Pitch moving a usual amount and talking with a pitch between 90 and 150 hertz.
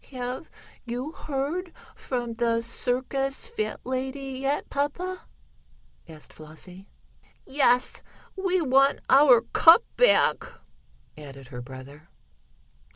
No: average, 4.1 semitones; very high, 260 Hz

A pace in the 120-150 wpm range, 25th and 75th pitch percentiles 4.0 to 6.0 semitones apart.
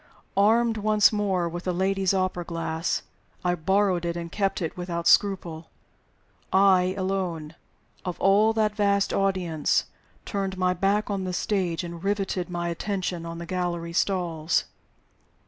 No: average, 145 wpm; narrow, 2.4 semitones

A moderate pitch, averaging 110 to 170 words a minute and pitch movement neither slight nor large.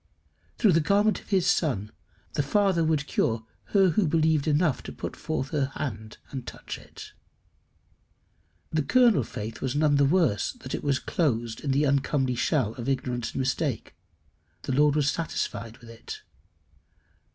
Yes: medium, 145 Hz; average, 165 wpm; average, 4.4 semitones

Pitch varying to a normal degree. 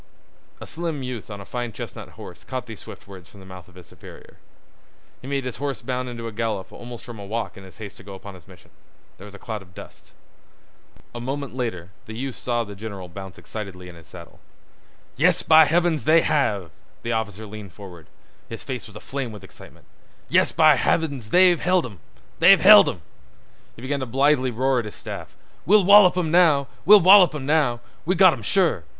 No: wide, 6.7 semitones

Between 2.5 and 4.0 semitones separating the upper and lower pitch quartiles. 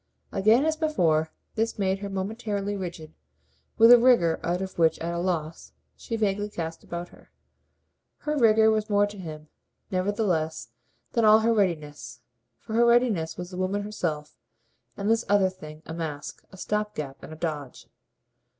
No: average, 4.9 semitones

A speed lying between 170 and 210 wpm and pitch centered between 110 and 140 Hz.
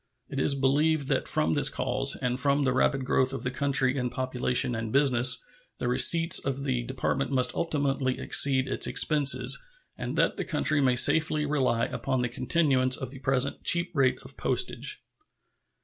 Yes: average, 175 wpm; low, 135 Hz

